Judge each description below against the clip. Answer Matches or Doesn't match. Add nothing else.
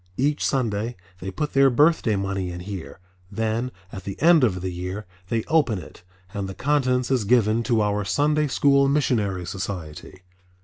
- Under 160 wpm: Doesn't match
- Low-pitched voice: Matches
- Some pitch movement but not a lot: Doesn't match